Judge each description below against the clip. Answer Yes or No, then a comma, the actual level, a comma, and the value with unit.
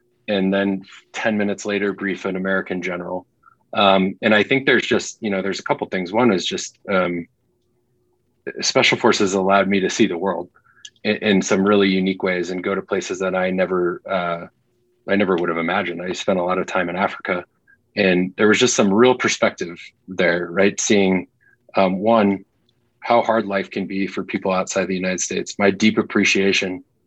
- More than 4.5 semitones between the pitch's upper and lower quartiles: No, narrow, 2.4 semitones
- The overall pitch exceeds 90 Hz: Yes, low, 100 Hz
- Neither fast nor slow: Yes, average, 195 wpm